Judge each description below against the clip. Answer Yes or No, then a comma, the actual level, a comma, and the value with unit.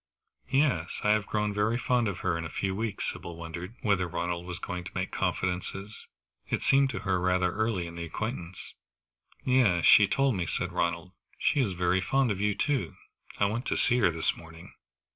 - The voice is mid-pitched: No, very low, 95 Hz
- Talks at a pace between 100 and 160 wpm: No, average, 200 wpm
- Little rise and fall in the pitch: No, average, 4.3 semitones